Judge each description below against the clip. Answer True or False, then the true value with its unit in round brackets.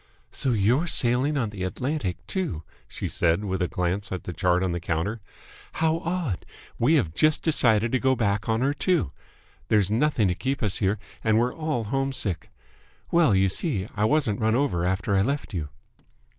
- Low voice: True (110 Hz)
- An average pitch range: False (6.4 semitones)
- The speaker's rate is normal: True (185 wpm)